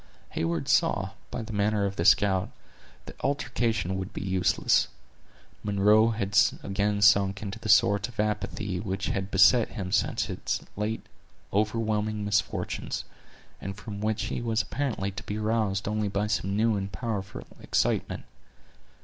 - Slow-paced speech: No, average, 150 wpm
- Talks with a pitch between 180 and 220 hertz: No, low, 105 Hz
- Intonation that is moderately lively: No, narrow, 1.9 semitones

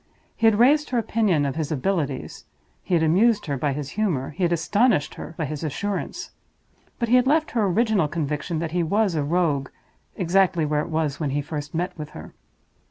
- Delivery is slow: No, fast, 205 wpm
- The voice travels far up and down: Yes, wide, 5.9 semitones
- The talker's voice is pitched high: No, medium, 170 Hz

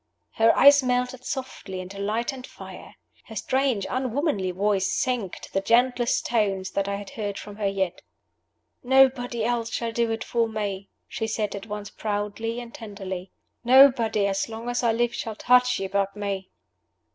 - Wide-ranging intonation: No, average, 3.5 semitones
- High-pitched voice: Yes, high, 225 Hz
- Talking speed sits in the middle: Yes, average, 170 wpm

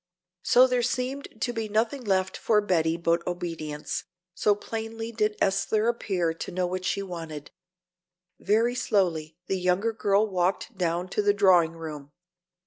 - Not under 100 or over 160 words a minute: Yes, average, 150 wpm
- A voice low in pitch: No, high, 195 Hz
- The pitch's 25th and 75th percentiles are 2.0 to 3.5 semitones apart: No, average, 4.3 semitones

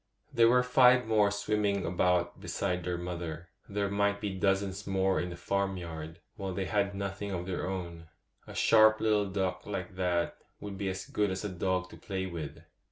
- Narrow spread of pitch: Yes, narrow, 2.3 semitones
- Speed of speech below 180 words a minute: No, average, 190 wpm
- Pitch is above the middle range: No, very low, 95 Hz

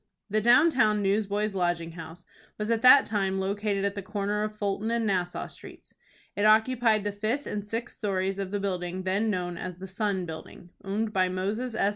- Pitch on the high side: Yes, high, 205 Hz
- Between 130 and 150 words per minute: No, average, 195 wpm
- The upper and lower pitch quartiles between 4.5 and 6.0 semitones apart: No, narrow, 2.5 semitones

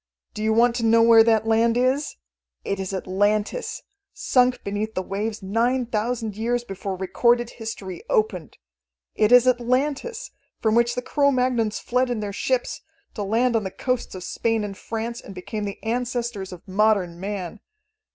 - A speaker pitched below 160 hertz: No, high, 225 Hz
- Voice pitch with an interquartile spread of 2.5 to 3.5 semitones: Yes, average, 3.1 semitones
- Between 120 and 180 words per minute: Yes, average, 170 wpm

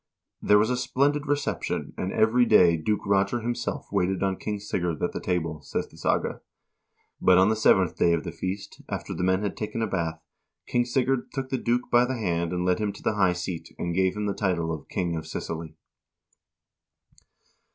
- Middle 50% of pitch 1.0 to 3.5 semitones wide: No, average, 4.4 semitones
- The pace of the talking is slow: No, fast, 205 wpm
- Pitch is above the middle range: No, very low, 95 Hz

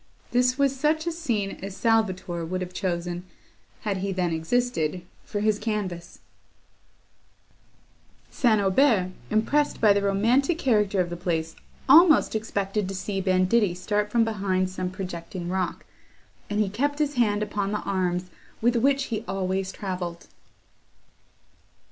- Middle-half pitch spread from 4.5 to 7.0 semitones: No, average, 3.9 semitones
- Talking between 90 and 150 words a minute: Yes, average, 140 wpm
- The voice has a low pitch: No, high, 200 Hz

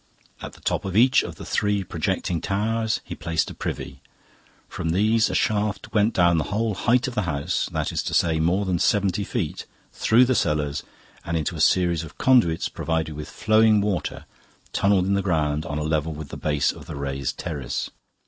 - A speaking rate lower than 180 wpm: No, average, 200 wpm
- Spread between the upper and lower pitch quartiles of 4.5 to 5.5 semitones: Yes, average, 5.1 semitones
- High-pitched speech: No, very low, 90 Hz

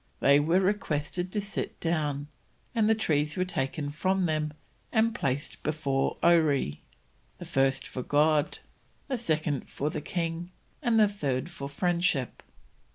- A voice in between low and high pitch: Yes, medium, 155 Hz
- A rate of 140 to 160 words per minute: Yes, average, 145 wpm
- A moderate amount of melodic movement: Yes, average, 4.3 semitones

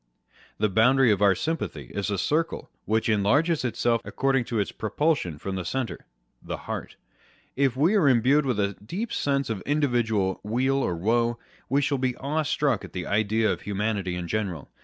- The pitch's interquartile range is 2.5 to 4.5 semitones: No, average, 5.3 semitones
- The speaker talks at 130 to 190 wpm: Yes, average, 180 wpm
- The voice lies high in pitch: No, low, 115 Hz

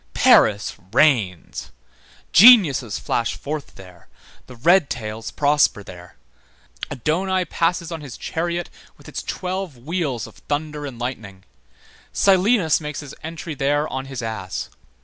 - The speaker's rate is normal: No, slow, 130 wpm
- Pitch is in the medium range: Yes, medium, 145 Hz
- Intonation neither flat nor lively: No, wide, 6.3 semitones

